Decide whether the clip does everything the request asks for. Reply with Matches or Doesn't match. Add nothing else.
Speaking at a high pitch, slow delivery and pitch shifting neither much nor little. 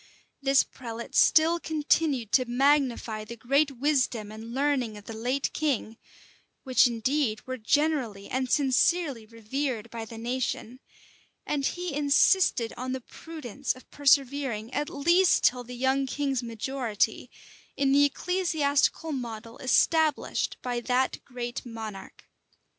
Matches